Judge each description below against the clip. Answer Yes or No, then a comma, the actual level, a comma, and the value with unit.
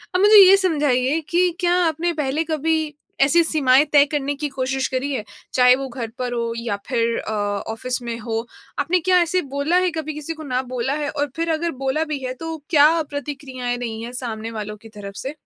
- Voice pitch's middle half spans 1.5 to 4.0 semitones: No, average, 4.4 semitones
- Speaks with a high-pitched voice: Yes, very high, 275 Hz